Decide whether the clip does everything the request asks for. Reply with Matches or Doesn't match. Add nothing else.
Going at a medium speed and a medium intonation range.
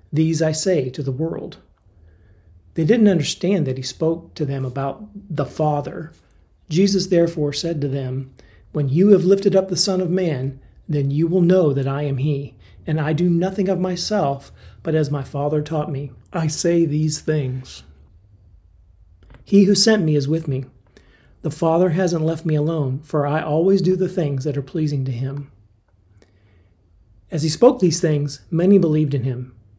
Matches